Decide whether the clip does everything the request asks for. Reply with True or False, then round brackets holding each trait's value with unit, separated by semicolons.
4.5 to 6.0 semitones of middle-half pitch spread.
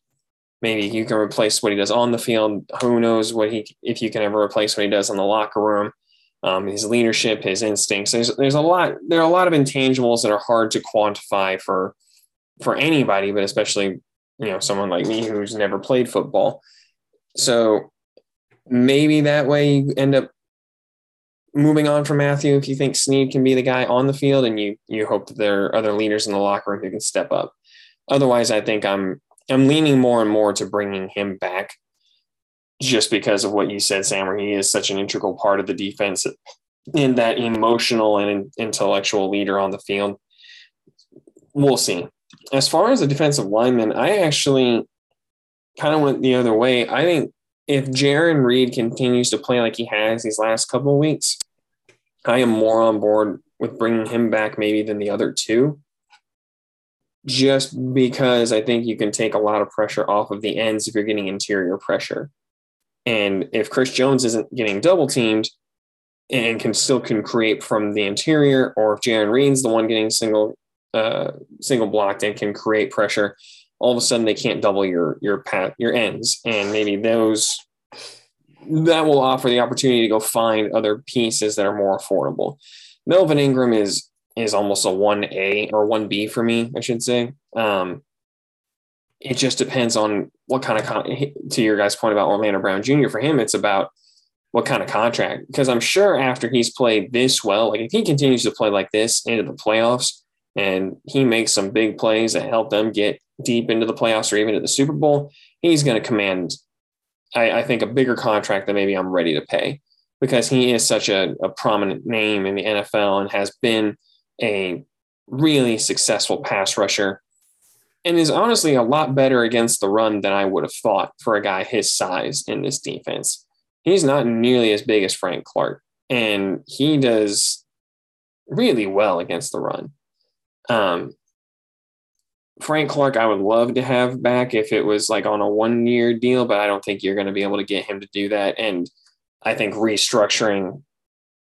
False (3.8 semitones)